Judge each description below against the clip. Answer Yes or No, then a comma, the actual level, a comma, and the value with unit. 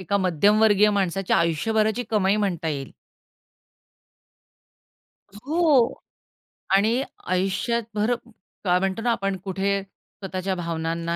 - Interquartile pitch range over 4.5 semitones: No, average, 3.0 semitones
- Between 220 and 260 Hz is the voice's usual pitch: No, high, 195 Hz